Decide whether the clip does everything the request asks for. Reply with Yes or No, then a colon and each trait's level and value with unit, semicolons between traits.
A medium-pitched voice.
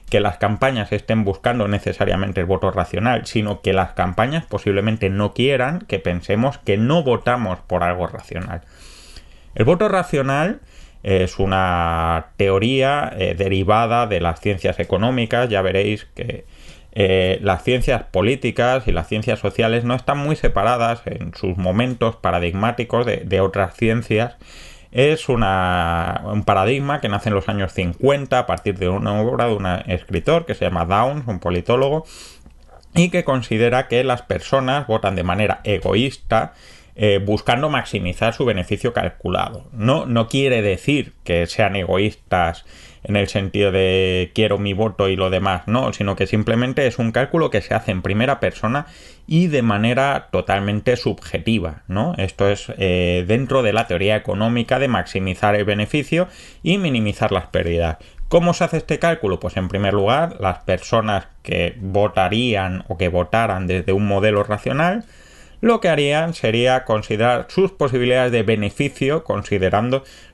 No: low, 105 Hz